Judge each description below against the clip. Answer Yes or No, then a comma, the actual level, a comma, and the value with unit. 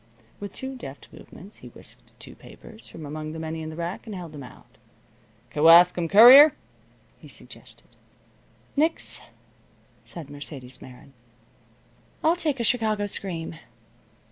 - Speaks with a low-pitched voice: No, medium, 170 Hz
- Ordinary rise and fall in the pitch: No, wide, 6.3 semitones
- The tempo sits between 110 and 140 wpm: Yes, slow, 135 wpm